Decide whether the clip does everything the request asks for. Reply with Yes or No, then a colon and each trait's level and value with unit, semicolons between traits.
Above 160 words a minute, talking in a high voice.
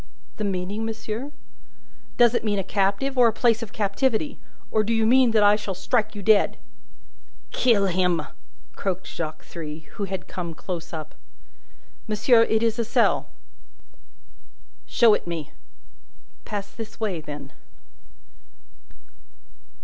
No: slow, 135 wpm; high, 210 Hz